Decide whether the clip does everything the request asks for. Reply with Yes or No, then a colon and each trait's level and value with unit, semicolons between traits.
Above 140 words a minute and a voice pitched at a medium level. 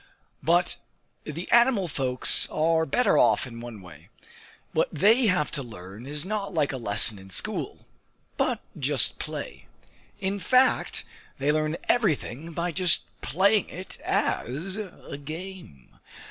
No: slow, 135 wpm; medium, 160 Hz